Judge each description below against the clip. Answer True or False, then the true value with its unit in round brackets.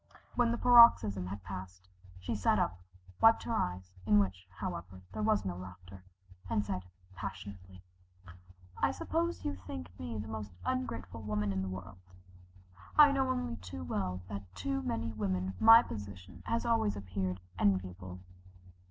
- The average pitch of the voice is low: True (95 Hz)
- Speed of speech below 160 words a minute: True (150 wpm)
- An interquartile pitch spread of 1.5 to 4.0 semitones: True (2.9 semitones)